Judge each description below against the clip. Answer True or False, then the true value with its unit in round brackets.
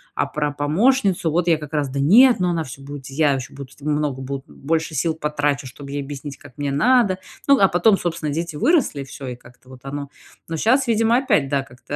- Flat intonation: False (4.3 semitones)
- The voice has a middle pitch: True (150 Hz)